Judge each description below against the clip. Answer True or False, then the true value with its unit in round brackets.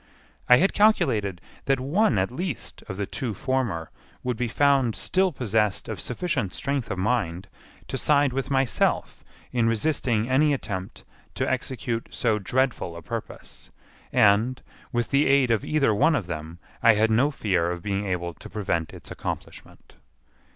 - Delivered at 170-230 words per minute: False (160 wpm)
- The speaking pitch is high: False (115 Hz)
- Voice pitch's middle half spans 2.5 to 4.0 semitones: False (5.3 semitones)